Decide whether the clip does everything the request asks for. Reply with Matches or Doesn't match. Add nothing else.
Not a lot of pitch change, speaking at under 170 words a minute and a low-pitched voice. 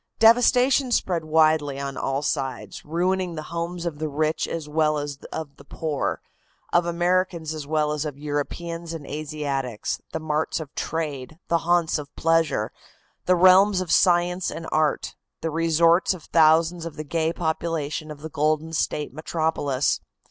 Doesn't match